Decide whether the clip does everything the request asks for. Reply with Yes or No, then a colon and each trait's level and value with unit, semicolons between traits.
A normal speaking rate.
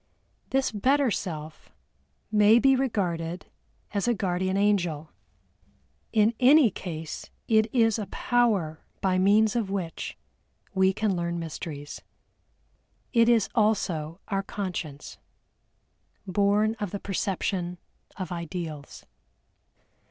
No: slow, 105 wpm